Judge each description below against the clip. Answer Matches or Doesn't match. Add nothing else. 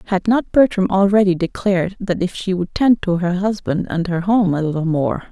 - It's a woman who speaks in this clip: Matches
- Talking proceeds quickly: Matches